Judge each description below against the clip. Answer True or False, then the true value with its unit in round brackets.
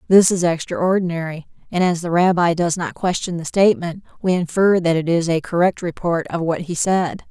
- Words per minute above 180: True (195 wpm)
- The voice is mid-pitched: True (170 Hz)